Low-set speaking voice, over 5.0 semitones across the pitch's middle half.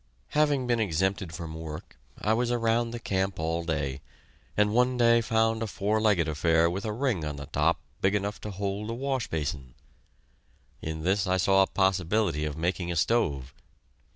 Yes: very low, 95 Hz; wide, 5.6 semitones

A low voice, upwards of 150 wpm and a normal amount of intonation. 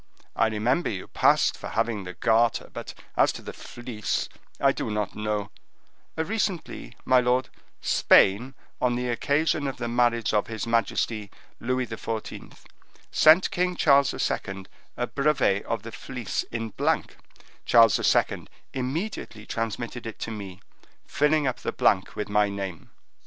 No: low, 115 Hz; average, 145 wpm; average, 3.5 semitones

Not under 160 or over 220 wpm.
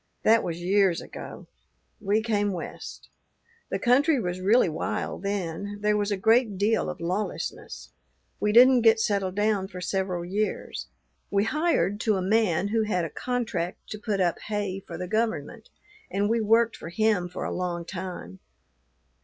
Yes: average, 165 wpm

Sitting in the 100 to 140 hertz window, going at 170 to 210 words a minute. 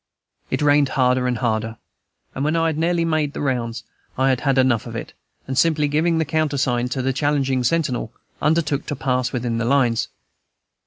Yes: low, 135 Hz; average, 190 wpm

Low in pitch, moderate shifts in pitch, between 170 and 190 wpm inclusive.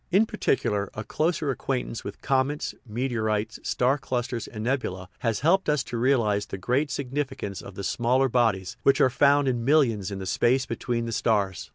Yes: low, 120 Hz; average, 4.3 semitones; average, 180 wpm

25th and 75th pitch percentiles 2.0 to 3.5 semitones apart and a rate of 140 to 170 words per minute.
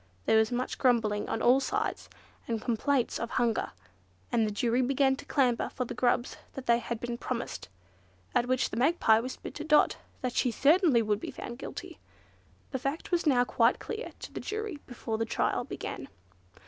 No: average, 2.8 semitones; average, 185 wpm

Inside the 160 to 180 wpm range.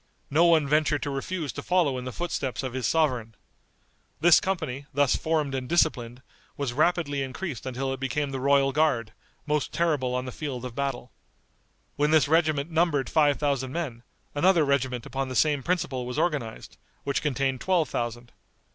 Yes: average, 175 wpm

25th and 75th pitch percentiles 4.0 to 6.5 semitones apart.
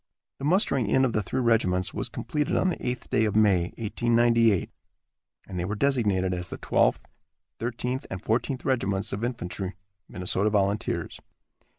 Yes: average, 4.3 semitones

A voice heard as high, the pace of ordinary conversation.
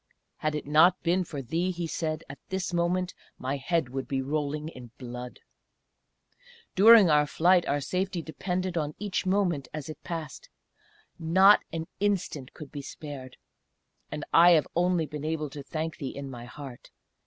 No: medium, 155 Hz; average, 165 wpm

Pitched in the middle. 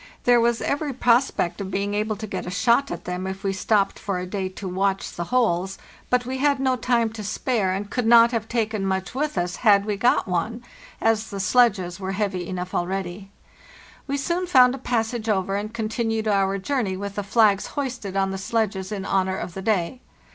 No: high, 205 Hz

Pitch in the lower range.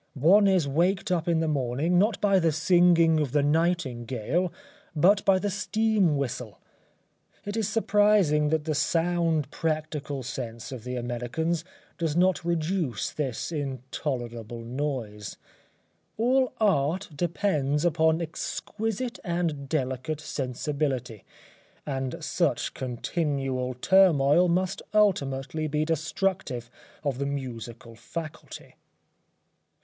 No: medium, 155 Hz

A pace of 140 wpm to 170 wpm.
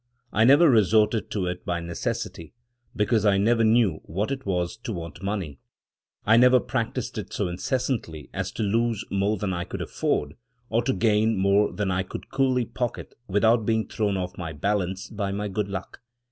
No: average, 185 wpm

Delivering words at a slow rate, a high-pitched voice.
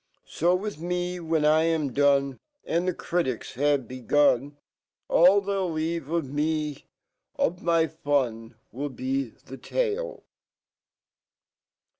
No: slow, 110 wpm; medium, 155 Hz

